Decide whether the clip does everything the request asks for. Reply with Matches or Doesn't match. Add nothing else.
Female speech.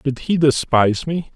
Doesn't match